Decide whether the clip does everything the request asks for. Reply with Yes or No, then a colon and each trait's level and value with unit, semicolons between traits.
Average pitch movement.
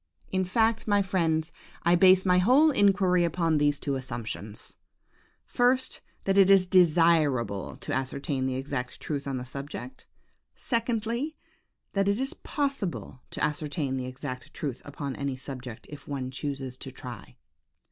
No: wide, 6.7 semitones